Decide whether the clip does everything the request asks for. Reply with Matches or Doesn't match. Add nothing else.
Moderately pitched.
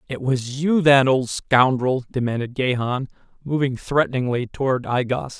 Doesn't match